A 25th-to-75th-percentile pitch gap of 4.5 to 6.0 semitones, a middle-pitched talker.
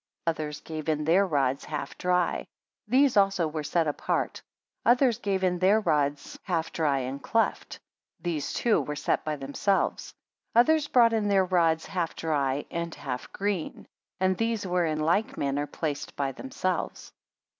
Yes: average, 5.1 semitones; medium, 165 Hz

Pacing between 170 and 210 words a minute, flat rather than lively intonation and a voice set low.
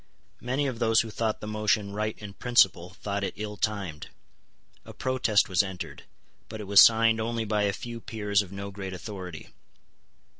Yes: average, 180 wpm; narrow, 2.3 semitones; low, 105 Hz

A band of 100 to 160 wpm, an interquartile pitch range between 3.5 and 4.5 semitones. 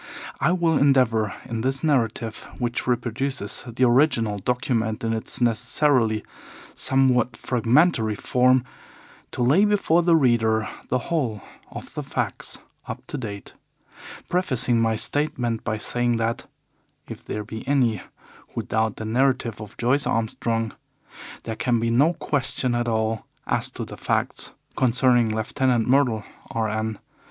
No: average, 140 wpm; average, 3.0 semitones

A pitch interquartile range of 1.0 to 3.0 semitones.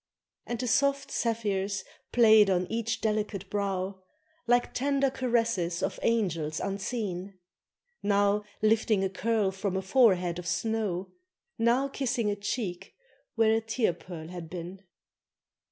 No: average, 3.5 semitones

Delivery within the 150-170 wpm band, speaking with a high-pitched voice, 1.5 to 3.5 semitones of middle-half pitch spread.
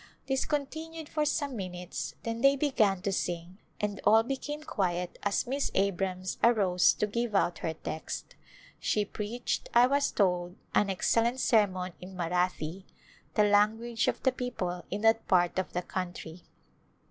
No: average, 160 wpm; high, 205 Hz; average, 5.0 semitones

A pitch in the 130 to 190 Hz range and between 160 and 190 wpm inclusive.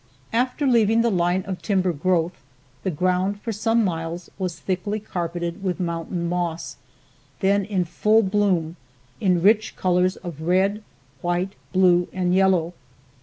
No: medium, 185 Hz; average, 140 wpm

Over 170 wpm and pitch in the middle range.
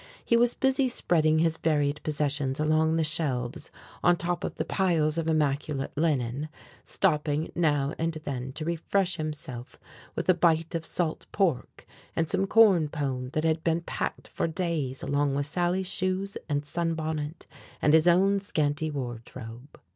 No: average, 155 wpm; medium, 155 Hz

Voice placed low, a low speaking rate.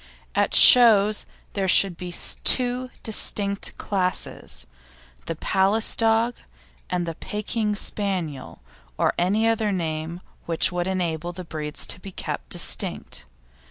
No: high, 190 Hz; slow, 125 wpm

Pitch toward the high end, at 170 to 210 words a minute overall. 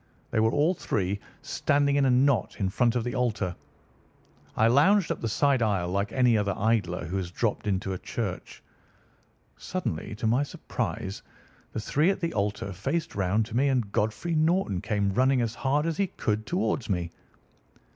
No: low, 115 Hz; average, 180 wpm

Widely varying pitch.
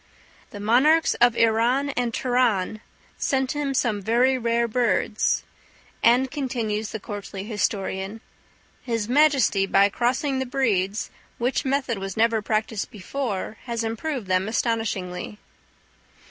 No: average, 3.7 semitones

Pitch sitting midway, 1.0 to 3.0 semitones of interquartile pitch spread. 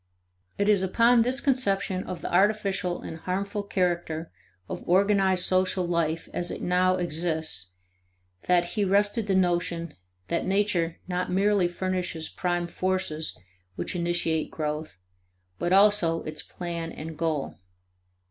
Yes: medium, 180 Hz; average, 2.7 semitones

